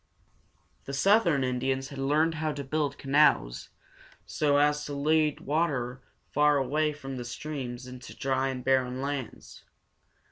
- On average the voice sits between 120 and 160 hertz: Yes, medium, 140 Hz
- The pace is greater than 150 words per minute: No, average, 145 wpm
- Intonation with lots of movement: No, narrow, 2.4 semitones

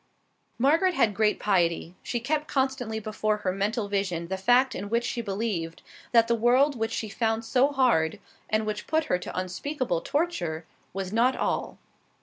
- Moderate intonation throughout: Yes, average, 4.8 semitones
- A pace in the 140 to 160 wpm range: No, average, 170 wpm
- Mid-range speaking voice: No, high, 220 Hz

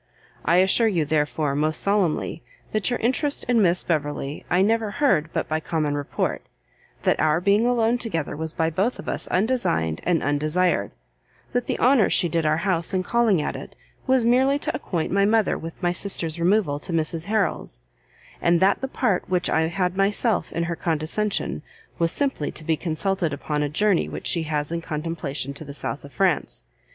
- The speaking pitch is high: No, medium, 175 Hz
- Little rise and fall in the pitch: No, average, 5.1 semitones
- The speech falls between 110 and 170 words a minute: No, average, 190 wpm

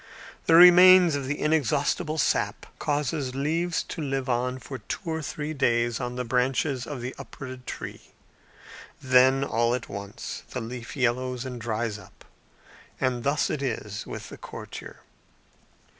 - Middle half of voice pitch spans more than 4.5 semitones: No, average, 3.4 semitones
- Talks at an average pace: Yes, average, 150 wpm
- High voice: No, low, 130 Hz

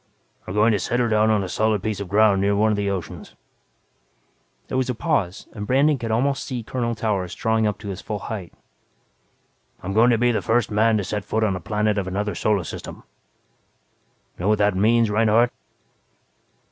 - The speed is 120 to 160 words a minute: No, average, 200 wpm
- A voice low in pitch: Yes, low, 110 Hz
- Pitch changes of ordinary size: No, narrow, 2.3 semitones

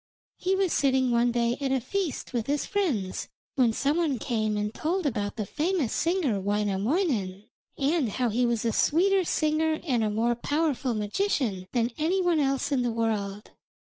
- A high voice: Yes, very high, 255 Hz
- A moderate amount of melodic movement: No, wide, 6.1 semitones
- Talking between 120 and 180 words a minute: Yes, average, 175 wpm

